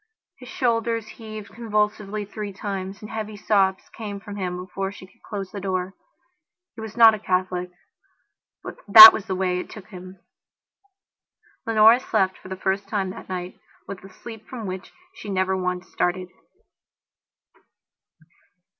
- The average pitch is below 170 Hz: No, high, 200 Hz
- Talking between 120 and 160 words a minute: Yes, average, 155 wpm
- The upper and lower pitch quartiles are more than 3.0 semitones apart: No, narrow, 2.5 semitones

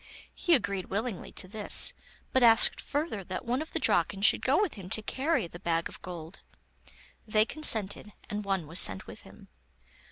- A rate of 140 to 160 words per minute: No, average, 185 wpm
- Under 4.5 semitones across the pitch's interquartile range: No, wide, 5.6 semitones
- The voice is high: Yes, high, 210 Hz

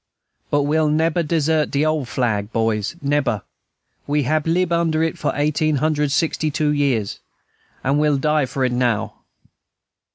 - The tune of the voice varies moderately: Yes, average, 3.2 semitones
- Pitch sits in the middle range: Yes, medium, 150 Hz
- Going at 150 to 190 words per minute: Yes, average, 155 wpm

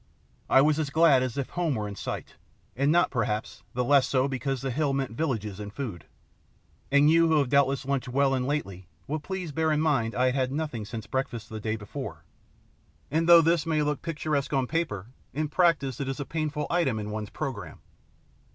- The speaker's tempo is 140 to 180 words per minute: No, fast, 205 wpm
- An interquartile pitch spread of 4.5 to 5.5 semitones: No, average, 4.1 semitones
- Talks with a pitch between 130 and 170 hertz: Yes, medium, 140 Hz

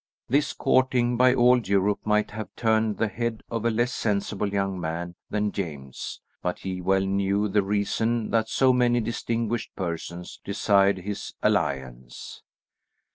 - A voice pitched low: Yes, low, 105 Hz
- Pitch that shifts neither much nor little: Yes, average, 3.4 semitones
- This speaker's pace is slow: No, average, 145 wpm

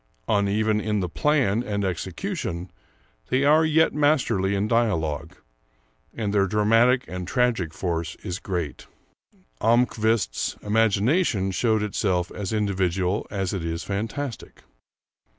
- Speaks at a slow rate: Yes, slow, 115 wpm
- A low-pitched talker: Yes, low, 105 Hz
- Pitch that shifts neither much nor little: Yes, average, 3.9 semitones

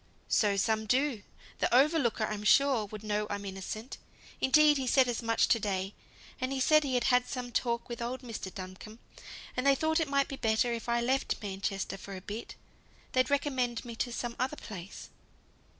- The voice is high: Yes, high, 235 Hz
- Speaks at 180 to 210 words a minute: Yes, average, 195 wpm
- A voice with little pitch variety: No, average, 3.8 semitones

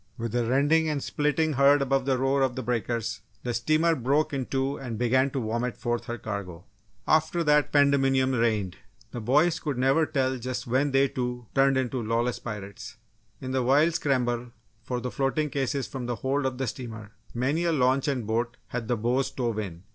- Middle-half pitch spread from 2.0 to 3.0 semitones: Yes, average, 2.7 semitones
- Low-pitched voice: Yes, low, 130 Hz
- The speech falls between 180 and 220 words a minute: Yes, average, 195 wpm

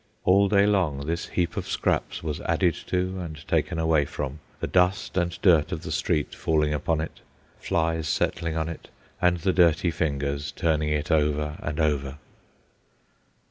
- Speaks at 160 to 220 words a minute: Yes, average, 165 wpm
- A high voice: No, very low, 80 Hz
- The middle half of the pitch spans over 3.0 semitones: No, narrow, 2.6 semitones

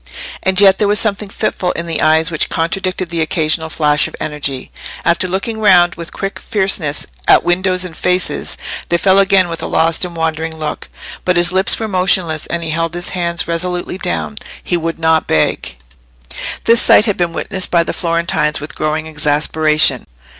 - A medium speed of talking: Yes, average, 180 wpm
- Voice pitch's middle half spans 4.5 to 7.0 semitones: No, average, 2.8 semitones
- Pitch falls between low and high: Yes, medium, 170 Hz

